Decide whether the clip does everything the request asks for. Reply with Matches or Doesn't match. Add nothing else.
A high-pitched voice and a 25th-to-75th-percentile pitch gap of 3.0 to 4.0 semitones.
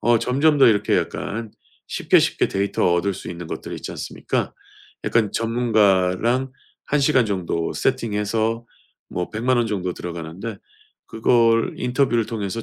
Doesn't match